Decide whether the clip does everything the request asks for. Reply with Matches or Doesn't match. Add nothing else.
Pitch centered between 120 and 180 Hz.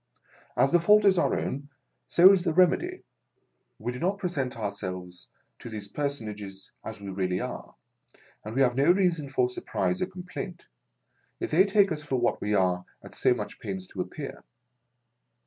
Matches